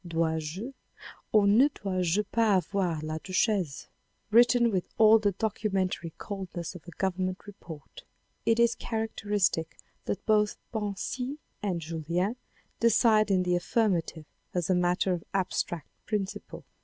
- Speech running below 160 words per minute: Yes, average, 145 wpm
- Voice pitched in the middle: No, high, 195 Hz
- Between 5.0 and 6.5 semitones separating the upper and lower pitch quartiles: No, average, 3.6 semitones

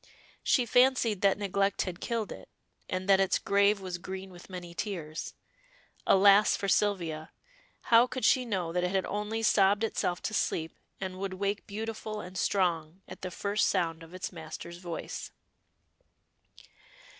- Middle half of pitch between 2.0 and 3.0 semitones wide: Yes, narrow, 2.5 semitones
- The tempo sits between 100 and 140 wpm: No, average, 155 wpm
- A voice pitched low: No, high, 195 Hz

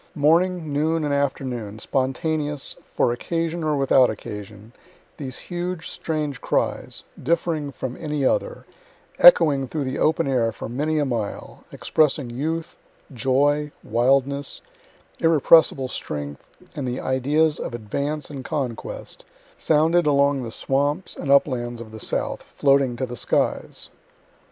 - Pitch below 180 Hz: Yes, medium, 140 Hz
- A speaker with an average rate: No, slow, 130 wpm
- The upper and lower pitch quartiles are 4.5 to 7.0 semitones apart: No, average, 3.6 semitones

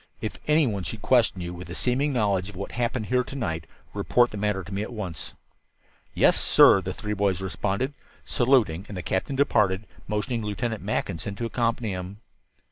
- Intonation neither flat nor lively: Yes, average, 4.1 semitones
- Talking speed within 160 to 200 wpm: Yes, average, 190 wpm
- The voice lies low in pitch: Yes, low, 105 Hz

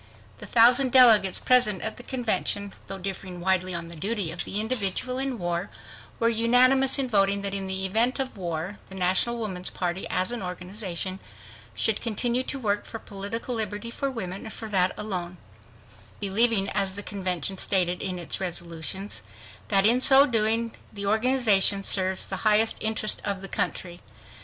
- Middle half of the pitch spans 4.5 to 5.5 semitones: No, average, 3.6 semitones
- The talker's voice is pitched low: No, high, 200 Hz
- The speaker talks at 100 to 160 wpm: No, average, 170 wpm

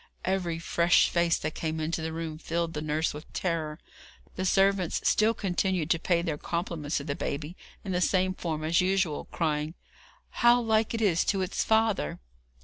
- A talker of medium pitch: Yes, medium, 170 Hz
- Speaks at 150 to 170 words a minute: No, average, 180 wpm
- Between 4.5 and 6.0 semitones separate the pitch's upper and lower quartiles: No, average, 3.2 semitones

